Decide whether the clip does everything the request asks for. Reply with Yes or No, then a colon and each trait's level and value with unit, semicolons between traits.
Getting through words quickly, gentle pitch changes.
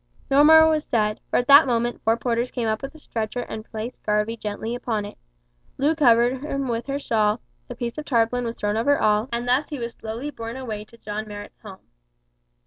No: fast, 220 wpm; average, 3.3 semitones